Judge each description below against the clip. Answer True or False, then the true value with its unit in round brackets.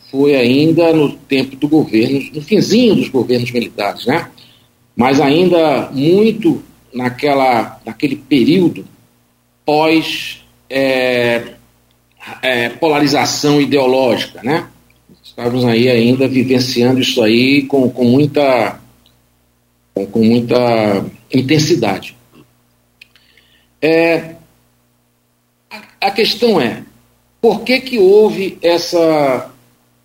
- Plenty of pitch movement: True (8.2 semitones)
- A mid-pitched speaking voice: False (130 Hz)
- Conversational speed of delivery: False (95 wpm)